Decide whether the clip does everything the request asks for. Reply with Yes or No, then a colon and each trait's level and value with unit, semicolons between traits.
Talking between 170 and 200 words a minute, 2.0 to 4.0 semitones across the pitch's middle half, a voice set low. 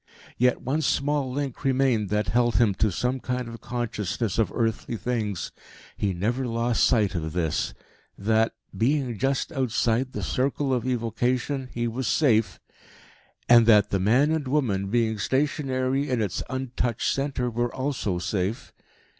No: average, 150 wpm; average, 3.3 semitones; low, 120 Hz